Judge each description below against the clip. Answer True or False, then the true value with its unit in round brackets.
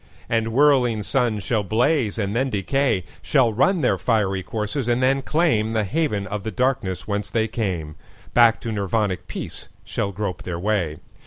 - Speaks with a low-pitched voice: True (110 Hz)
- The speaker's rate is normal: True (155 wpm)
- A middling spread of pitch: True (3.9 semitones)